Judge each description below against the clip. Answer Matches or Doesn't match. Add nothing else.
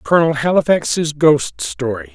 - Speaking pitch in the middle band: Matches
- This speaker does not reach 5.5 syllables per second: Matches